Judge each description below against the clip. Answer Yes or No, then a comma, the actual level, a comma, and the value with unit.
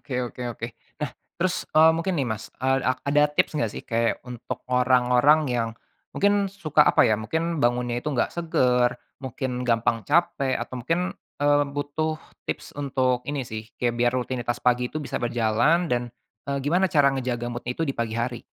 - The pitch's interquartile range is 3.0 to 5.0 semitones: Yes, average, 3.7 semitones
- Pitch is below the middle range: Yes, low, 130 Hz